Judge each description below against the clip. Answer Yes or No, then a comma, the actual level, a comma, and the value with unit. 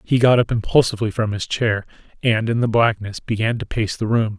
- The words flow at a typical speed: No, fast, 220 wpm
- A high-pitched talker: No, low, 110 Hz